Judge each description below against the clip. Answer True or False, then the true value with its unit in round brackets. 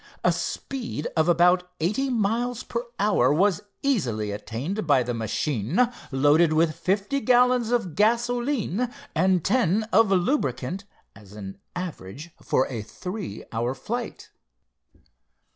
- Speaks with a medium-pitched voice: True (180 Hz)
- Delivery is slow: True (125 wpm)